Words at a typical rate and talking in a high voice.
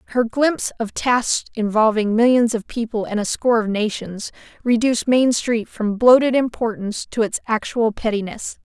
Yes: average, 160 wpm; high, 225 Hz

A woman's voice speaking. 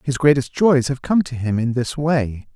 No: male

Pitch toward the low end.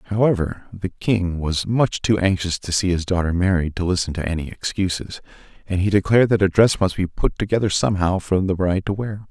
Yes: very low, 95 Hz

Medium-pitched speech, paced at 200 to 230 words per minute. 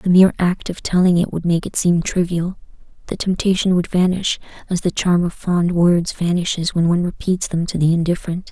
Yes: medium, 175 Hz; fast, 205 wpm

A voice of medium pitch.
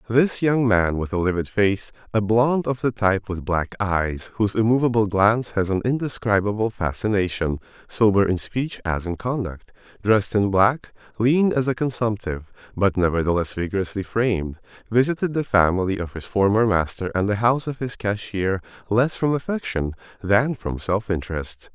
No: low, 105 Hz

